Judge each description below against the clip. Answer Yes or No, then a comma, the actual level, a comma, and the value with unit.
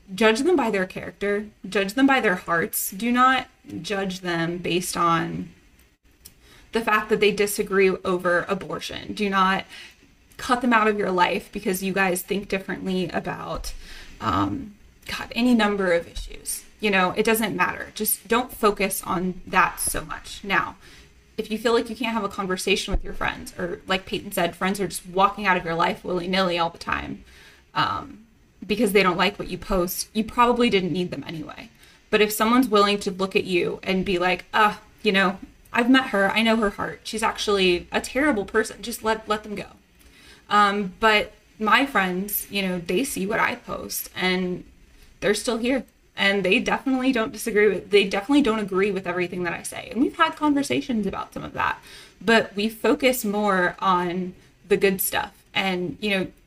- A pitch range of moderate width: Yes, average, 3.1 semitones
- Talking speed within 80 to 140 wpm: No, average, 190 wpm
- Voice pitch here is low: No, high, 200 Hz